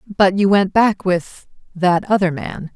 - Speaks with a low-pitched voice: No, high, 190 Hz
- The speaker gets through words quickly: No, average, 155 wpm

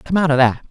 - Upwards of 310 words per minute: Yes, fast, 340 wpm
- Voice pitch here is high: No, medium, 150 Hz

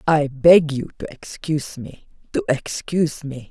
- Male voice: No, female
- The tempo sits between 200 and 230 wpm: No, average, 155 wpm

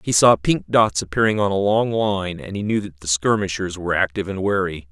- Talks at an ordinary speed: No, fast, 230 wpm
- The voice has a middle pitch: No, low, 100 Hz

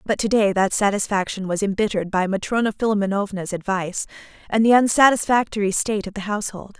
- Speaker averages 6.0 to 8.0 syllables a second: Yes, 6.4 syllables/s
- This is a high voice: Yes, high, 205 Hz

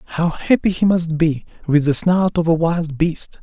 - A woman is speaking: No, male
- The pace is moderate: No, fast, 210 wpm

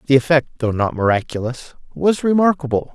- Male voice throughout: Yes, male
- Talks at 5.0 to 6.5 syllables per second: Yes, 5.8 syllables/s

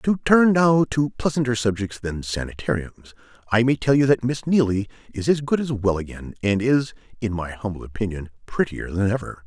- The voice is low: Yes, low, 115 Hz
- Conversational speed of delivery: Yes, average, 190 wpm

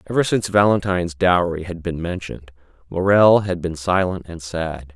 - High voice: No, very low, 90 Hz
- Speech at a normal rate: Yes, average, 155 wpm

